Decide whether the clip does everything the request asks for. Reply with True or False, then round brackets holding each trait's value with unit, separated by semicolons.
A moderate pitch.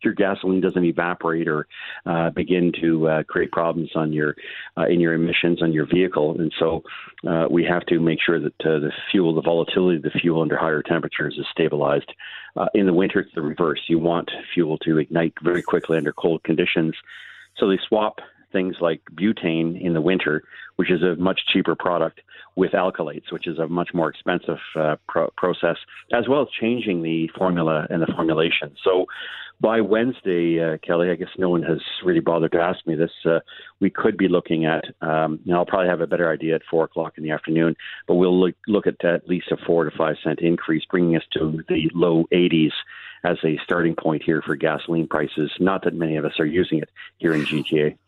False (85 Hz)